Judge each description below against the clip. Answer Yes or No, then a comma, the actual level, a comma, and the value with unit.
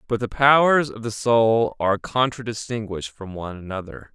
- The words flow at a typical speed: Yes, average, 160 wpm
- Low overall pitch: Yes, low, 115 Hz